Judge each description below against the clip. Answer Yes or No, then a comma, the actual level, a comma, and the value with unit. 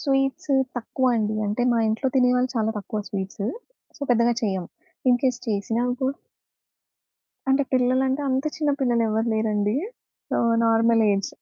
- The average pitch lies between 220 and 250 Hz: Yes, high, 235 Hz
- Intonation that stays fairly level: No, average, 3.3 semitones